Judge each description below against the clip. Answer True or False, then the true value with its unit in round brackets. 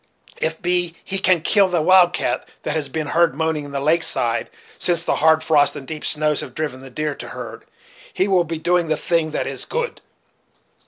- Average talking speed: False (220 wpm)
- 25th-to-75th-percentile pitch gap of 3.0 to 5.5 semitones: False (2.5 semitones)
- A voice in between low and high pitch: True (160 Hz)